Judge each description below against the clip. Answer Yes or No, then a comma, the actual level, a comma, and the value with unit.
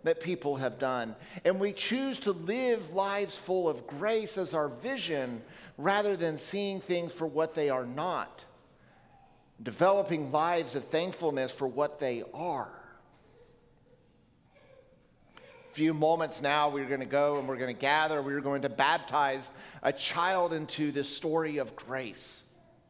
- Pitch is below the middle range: No, medium, 160 Hz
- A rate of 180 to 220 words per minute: No, average, 145 wpm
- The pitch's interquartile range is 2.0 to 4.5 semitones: No, average, 5.1 semitones